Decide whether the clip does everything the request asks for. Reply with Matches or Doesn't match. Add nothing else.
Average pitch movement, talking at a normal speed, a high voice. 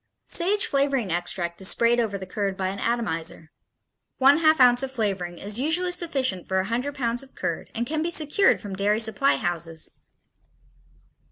Doesn't match